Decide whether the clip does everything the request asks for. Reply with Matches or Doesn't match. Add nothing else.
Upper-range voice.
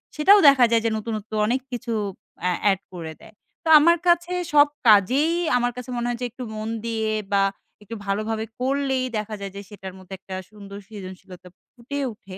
Matches